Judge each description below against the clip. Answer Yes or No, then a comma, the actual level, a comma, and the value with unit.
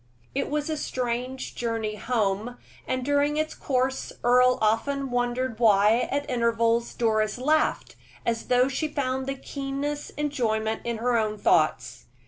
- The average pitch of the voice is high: Yes, high, 245 Hz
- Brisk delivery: No, average, 140 wpm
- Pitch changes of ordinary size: Yes, average, 3.4 semitones